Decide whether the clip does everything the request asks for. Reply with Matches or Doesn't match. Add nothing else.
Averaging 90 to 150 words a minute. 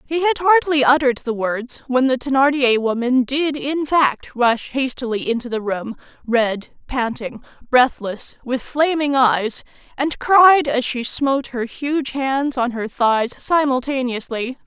Matches